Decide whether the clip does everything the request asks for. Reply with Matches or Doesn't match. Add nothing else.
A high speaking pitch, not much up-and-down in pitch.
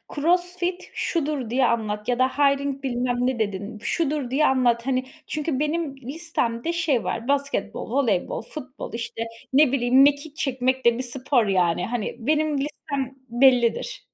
Doesn't match